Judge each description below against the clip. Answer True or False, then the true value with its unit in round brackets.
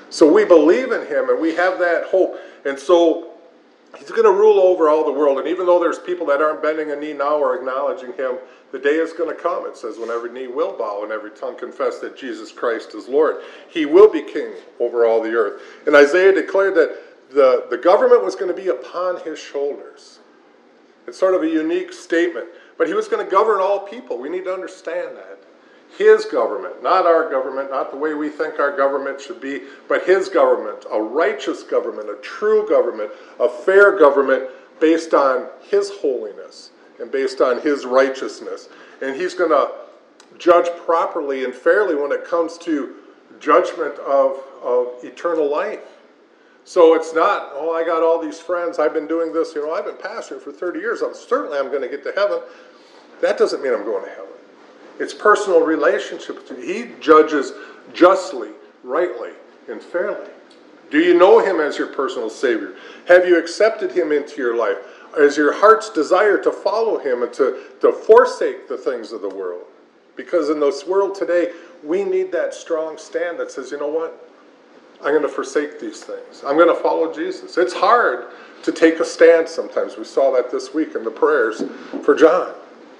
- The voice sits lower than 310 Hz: False (375 Hz)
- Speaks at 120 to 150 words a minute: False (195 wpm)